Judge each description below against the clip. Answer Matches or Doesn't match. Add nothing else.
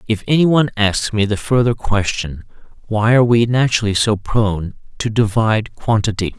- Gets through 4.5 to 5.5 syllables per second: Matches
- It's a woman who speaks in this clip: Doesn't match